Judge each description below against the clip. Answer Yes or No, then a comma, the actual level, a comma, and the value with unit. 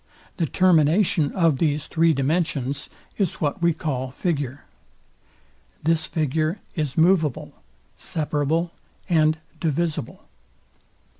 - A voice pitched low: No, medium, 155 Hz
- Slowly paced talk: Yes, slow, 95 wpm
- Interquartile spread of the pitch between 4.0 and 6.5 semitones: No, average, 2.7 semitones